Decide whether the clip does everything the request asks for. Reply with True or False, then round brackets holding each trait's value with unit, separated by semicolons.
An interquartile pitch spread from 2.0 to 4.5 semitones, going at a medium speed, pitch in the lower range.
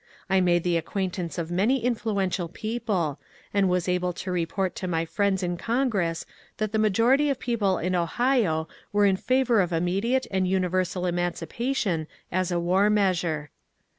False (3.6 semitones; 165 wpm; 185 Hz)